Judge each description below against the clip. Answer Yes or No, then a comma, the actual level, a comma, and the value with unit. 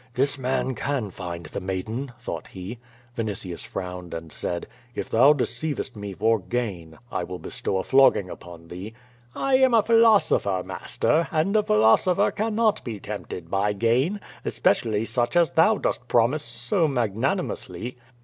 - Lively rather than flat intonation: Yes, wide, 7.7 semitones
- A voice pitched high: No, low, 115 Hz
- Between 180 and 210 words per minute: No, average, 160 wpm